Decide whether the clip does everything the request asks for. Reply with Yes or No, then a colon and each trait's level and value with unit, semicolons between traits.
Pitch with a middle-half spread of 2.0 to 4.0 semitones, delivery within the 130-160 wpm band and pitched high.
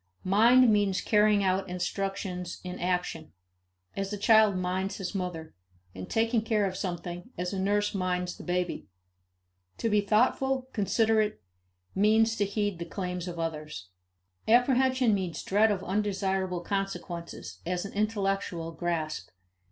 Yes: average, 2.9 semitones; average, 140 wpm; high, 195 Hz